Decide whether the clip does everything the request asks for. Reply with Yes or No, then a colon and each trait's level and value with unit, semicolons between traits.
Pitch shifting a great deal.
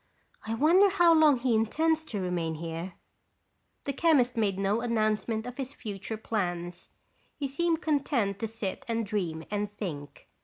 Yes: wide, 6.1 semitones